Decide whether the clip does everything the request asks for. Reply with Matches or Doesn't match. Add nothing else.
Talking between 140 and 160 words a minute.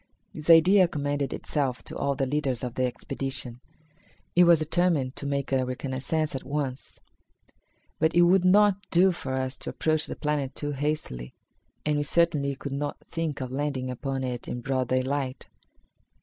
Doesn't match